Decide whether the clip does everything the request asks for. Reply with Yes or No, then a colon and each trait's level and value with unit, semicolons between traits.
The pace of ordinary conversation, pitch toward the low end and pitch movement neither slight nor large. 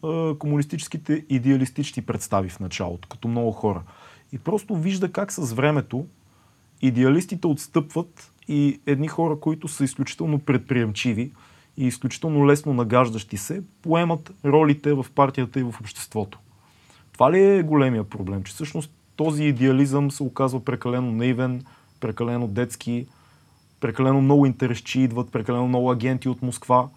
Yes: average, 130 wpm; low, 130 Hz; average, 3.6 semitones